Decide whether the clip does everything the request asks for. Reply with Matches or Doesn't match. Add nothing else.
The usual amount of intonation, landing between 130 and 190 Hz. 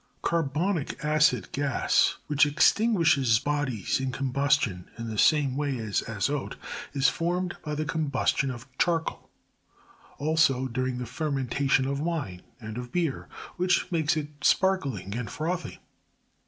Matches